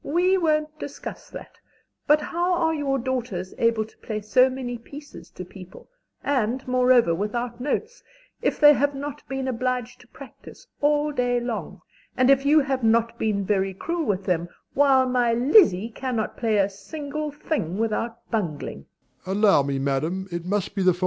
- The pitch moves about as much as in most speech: Yes, average, 4.6 semitones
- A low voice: No, very high, 250 Hz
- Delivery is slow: No, average, 150 wpm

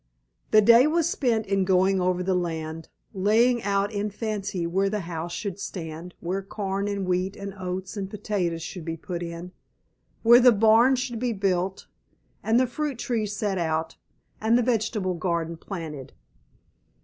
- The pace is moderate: Yes, average, 165 wpm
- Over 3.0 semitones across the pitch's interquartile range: Yes, average, 3.7 semitones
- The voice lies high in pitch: Yes, high, 195 Hz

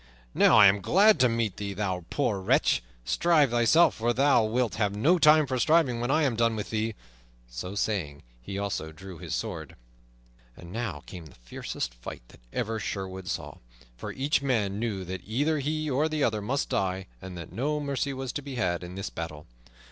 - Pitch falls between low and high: No, low, 110 Hz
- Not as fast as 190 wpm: No, average, 200 wpm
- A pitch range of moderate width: No, wide, 6.5 semitones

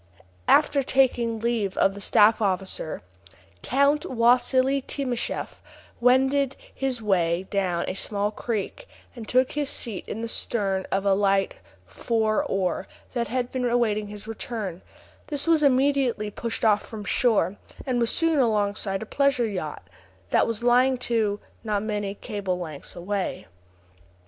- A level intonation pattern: No, average, 4.1 semitones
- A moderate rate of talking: Yes, average, 145 wpm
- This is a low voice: No, high, 225 Hz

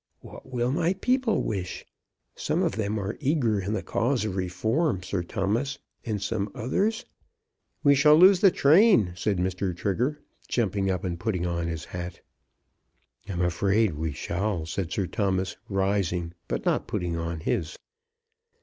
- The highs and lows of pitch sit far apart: Yes, wide, 6.3 semitones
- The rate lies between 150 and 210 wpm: Yes, average, 160 wpm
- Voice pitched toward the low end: Yes, low, 100 Hz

